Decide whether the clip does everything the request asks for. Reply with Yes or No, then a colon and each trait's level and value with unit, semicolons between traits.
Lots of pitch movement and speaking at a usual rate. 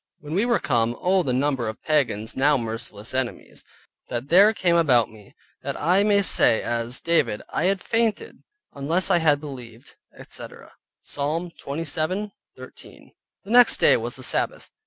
Yes: wide, 7.2 semitones; average, 155 wpm